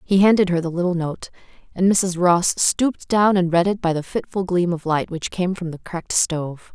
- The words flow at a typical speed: No, fast, 230 wpm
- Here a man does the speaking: No, female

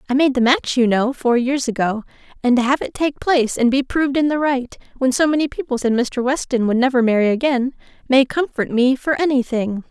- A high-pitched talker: Yes, very high, 260 Hz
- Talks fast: Yes, fast, 230 wpm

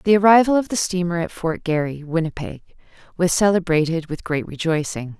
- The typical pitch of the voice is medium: Yes, medium, 170 Hz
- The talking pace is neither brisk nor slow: Yes, average, 160 wpm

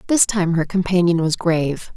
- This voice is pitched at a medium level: Yes, medium, 175 Hz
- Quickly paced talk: No, average, 185 wpm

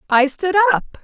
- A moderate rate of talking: Yes, average, 175 wpm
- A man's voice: No, female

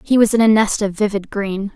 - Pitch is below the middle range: No, high, 205 Hz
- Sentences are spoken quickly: Yes, fast, 275 wpm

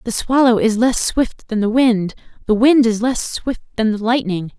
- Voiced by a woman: Yes, female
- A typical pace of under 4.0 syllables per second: No, 4.6 syllables/s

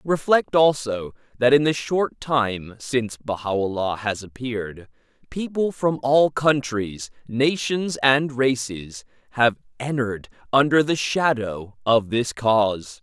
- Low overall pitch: Yes, low, 125 Hz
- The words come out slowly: Yes, slow, 120 wpm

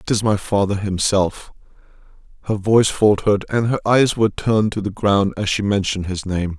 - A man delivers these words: Yes, male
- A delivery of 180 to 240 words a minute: Yes, average, 190 wpm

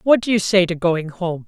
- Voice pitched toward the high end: No, medium, 180 Hz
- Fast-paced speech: Yes, fast, 285 wpm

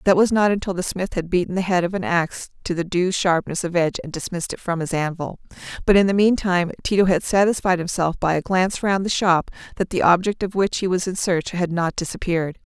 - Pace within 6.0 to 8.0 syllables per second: Yes, 6.1 syllables/s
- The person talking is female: Yes, female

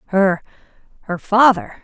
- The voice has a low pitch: No, high, 210 Hz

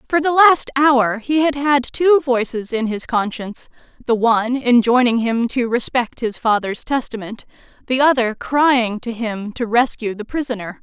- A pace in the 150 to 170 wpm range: Yes, average, 165 wpm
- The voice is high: Yes, high, 245 Hz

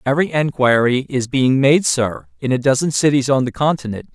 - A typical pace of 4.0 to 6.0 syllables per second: Yes, 5.5 syllables/s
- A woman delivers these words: No, male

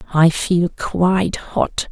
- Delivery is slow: Yes, slow, 125 wpm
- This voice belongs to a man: No, female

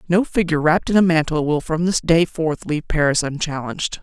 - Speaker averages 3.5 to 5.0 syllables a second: No, 6.0 syllables/s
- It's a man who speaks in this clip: No, female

